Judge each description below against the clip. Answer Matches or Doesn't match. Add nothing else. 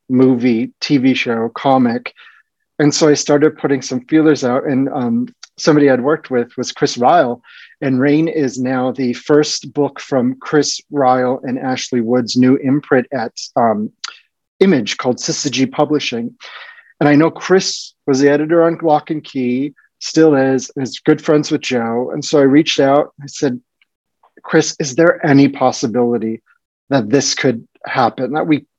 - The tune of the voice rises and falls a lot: Doesn't match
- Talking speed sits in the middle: Matches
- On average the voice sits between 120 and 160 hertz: Matches